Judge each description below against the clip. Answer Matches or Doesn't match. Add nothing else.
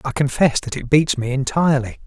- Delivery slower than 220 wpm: Matches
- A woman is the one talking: Doesn't match